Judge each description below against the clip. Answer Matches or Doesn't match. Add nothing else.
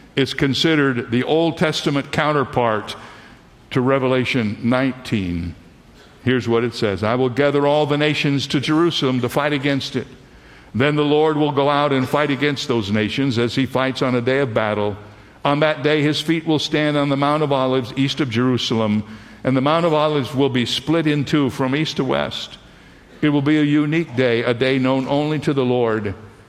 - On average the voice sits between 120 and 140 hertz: Matches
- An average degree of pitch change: Matches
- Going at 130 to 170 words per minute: Doesn't match